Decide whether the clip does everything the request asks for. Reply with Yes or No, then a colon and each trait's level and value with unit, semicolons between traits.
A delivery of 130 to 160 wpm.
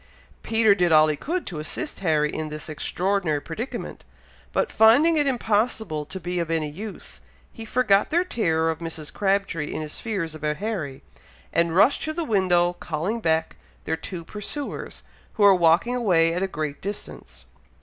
No: average, 170 wpm